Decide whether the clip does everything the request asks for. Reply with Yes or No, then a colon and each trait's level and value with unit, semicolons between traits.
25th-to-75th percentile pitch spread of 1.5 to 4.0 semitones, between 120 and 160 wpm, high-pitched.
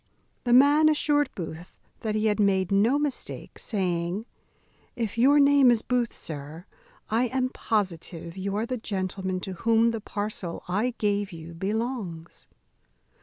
No: average, 4.7 semitones; average, 145 wpm; high, 210 Hz